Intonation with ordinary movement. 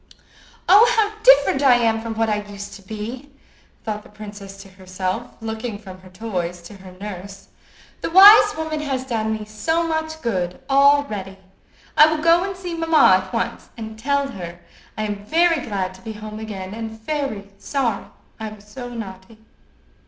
No: wide, 6.1 semitones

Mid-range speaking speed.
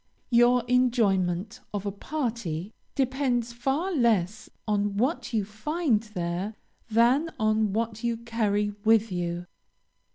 No: slow, 120 wpm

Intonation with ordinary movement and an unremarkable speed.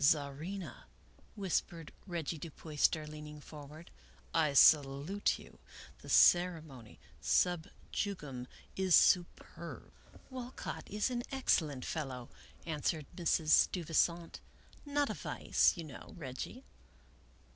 No: average, 3.6 semitones; slow, 120 wpm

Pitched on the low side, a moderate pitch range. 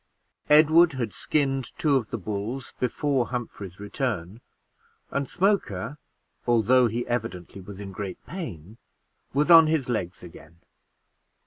No: low, 120 Hz; wide, 5.9 semitones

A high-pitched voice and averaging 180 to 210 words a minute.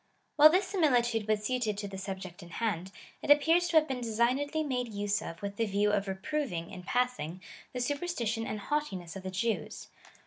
Yes: high, 225 Hz; average, 200 wpm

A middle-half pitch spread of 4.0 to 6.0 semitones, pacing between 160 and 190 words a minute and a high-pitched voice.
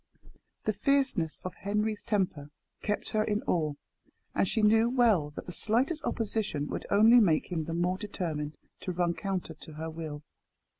Yes: average, 5.1 semitones; average, 165 wpm; high, 195 Hz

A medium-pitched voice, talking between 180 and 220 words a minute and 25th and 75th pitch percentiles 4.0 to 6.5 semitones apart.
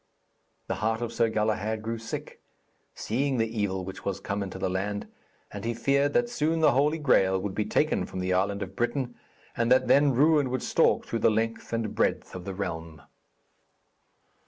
No: low, 110 Hz; average, 190 wpm; average, 4.7 semitones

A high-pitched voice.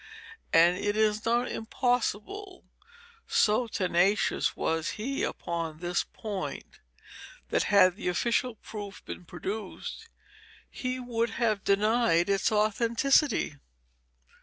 Yes: high, 210 Hz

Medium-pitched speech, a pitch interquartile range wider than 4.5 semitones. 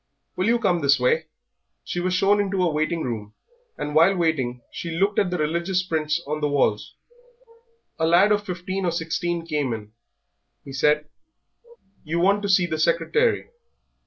No: medium, 170 Hz; average, 3.5 semitones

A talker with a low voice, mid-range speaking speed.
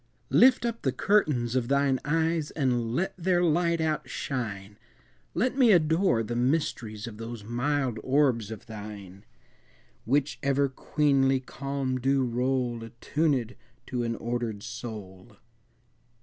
No: low, 130 Hz; slow, 130 wpm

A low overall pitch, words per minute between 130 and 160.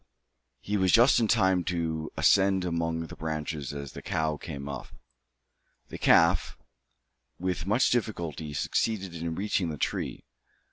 Yes: very low, 85 Hz; average, 140 wpm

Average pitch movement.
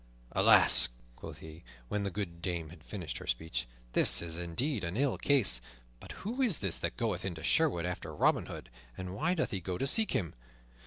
No: wide, 8.4 semitones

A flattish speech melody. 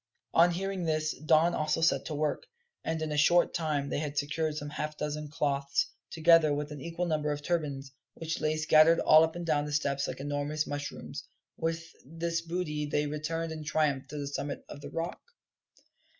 Yes: narrow, 1.9 semitones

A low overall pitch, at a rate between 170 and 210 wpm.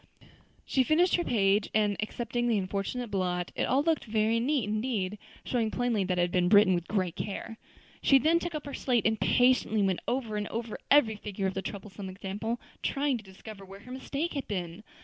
No: high, 215 Hz; fast, 205 wpm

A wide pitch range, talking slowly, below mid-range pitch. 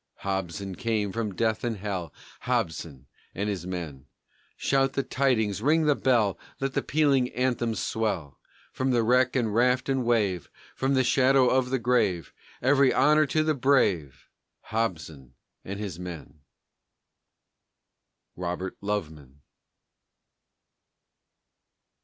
Yes: wide, 6.2 semitones; slow, 125 wpm; low, 110 Hz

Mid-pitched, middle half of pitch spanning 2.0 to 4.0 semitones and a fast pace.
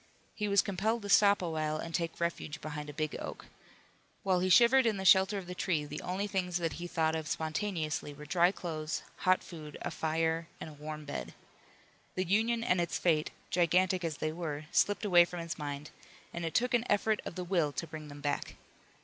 Yes: medium, 170 Hz; average, 3.7 semitones; fast, 215 wpm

